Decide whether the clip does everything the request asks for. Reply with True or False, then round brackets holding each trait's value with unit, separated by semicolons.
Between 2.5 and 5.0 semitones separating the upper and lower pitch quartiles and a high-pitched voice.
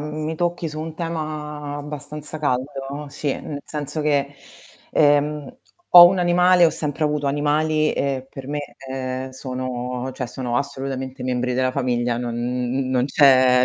False (2.9 semitones; 140 Hz)